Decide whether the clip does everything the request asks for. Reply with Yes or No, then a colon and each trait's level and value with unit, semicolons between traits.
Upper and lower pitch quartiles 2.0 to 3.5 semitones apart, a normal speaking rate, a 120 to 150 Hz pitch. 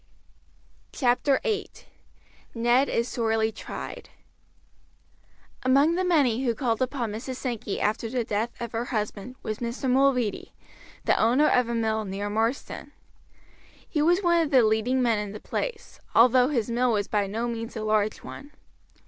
No: average, 3.1 semitones; average, 155 wpm; high, 235 Hz